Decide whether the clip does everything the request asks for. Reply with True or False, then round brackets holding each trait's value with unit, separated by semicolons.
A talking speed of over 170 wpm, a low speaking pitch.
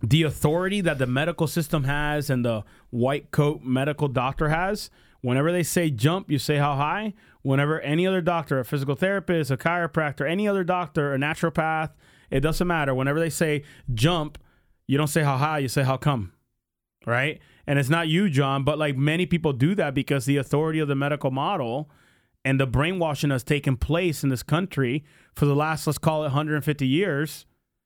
False (190 wpm; 150 Hz)